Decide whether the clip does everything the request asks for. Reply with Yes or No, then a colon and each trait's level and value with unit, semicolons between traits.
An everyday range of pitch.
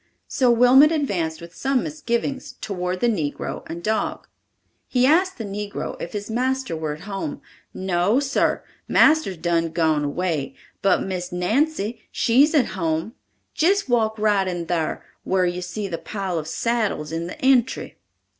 No: wide, 6.6 semitones